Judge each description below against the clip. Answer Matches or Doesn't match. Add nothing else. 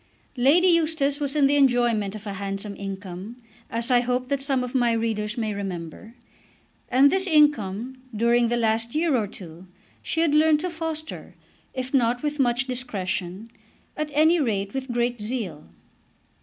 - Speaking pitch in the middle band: Doesn't match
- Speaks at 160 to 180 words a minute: Matches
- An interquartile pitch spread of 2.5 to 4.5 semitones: Doesn't match